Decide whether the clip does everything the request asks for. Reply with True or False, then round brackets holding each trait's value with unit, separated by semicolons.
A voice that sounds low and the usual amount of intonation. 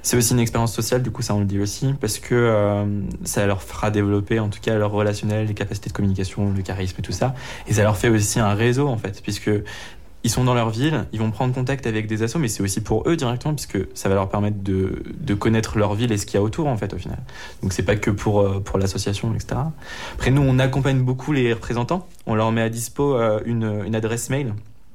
True (110 Hz; 3.3 semitones)